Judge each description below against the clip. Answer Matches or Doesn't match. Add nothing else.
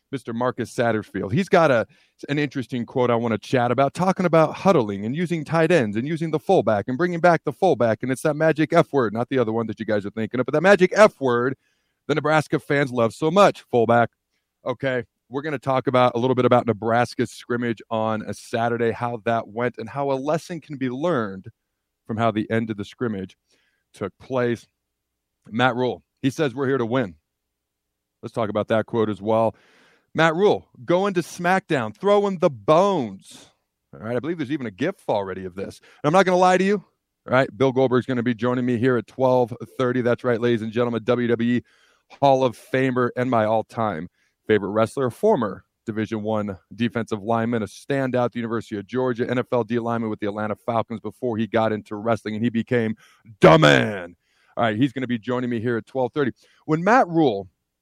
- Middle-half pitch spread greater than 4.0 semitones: Doesn't match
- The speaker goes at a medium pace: Doesn't match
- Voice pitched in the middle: Doesn't match